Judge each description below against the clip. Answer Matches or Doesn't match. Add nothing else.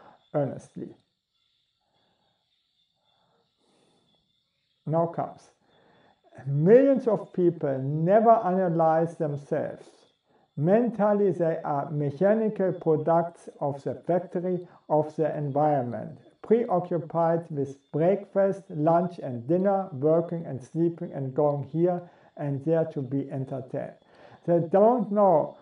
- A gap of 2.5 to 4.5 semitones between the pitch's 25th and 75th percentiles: Matches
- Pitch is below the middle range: Doesn't match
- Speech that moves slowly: Matches